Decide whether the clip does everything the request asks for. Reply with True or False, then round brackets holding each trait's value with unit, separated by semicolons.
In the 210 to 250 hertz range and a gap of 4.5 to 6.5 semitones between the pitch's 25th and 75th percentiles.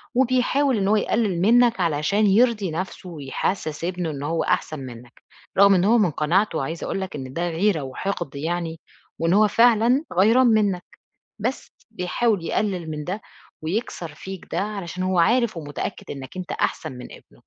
False (185 Hz; 5.0 semitones)